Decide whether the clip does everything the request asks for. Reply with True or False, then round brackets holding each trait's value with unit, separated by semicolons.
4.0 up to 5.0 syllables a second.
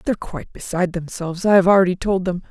False (7.3 syllables/s)